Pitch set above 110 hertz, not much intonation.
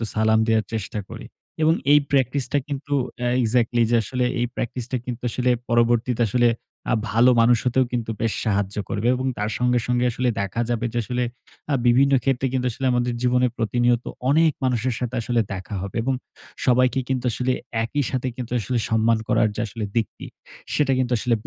Yes: low, 120 Hz; narrow, 2.0 semitones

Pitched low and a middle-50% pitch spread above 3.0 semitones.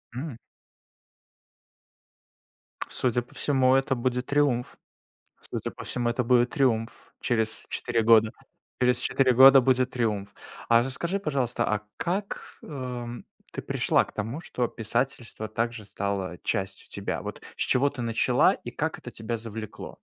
No: low, 120 Hz; average, 2.7 semitones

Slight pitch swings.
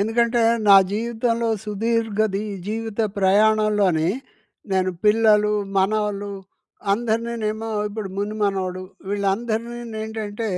Yes: narrow, 2.0 semitones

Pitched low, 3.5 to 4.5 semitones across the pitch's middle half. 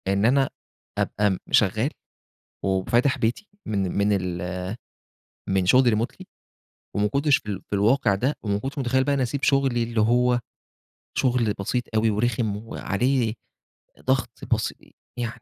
Yes: low, 115 Hz; average, 4.1 semitones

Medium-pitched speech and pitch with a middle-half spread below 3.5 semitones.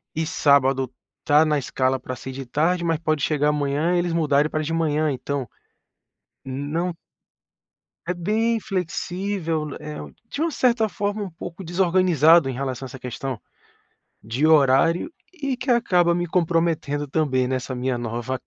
No: medium, 155 Hz; average, 4.5 semitones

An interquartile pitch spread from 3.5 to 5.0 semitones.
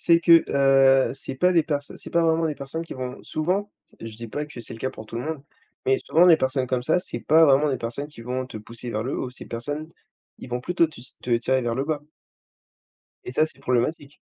Yes: average, 4.0 semitones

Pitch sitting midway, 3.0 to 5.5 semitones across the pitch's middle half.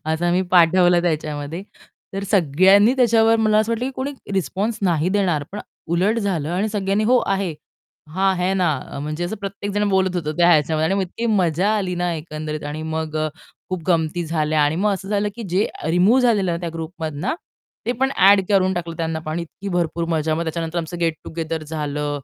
Yes: medium, 175 Hz; average, 3.8 semitones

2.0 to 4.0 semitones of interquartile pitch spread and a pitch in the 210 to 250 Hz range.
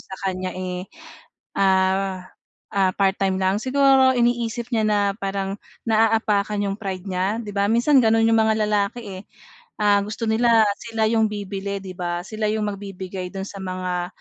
No: average, 2.8 semitones; high, 200 Hz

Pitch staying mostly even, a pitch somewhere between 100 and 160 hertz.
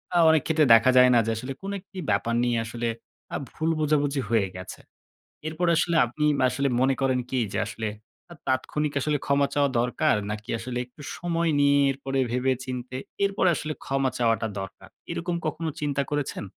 No: average, 3.7 semitones; low, 135 Hz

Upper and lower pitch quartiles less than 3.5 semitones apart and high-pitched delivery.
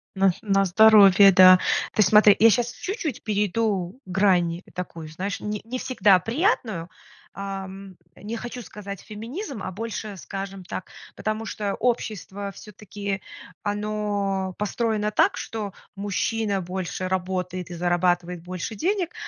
Yes: average, 2.7 semitones; high, 200 Hz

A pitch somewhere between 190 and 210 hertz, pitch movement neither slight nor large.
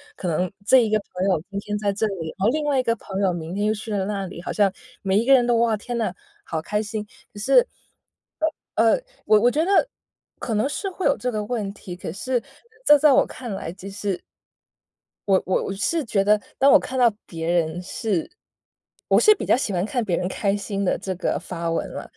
Yes: high, 205 Hz; average, 4.0 semitones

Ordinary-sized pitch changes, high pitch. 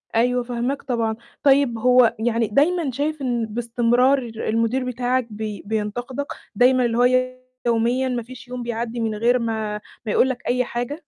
No: narrow, 1.9 semitones; high, 240 Hz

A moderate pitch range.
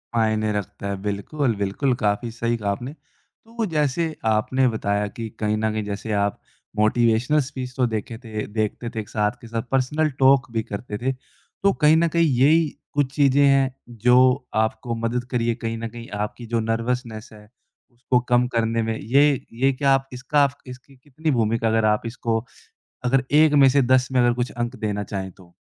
Yes: average, 3.3 semitones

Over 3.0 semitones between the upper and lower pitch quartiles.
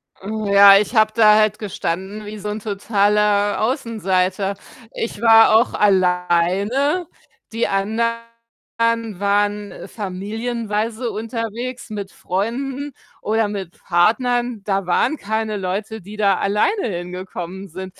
No: narrow, 2.5 semitones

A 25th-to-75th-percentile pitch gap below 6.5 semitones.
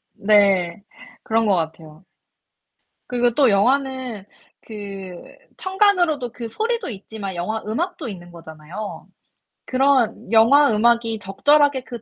Yes: average, 5.3 semitones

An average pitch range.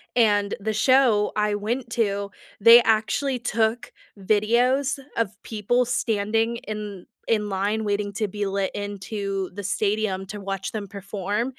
No: narrow, 2.3 semitones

